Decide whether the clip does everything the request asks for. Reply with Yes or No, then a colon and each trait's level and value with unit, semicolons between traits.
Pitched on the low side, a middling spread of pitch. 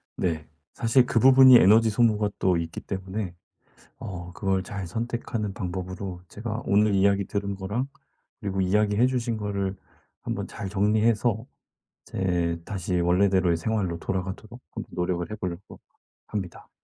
Yes: low, 100 Hz; average, 3.0 semitones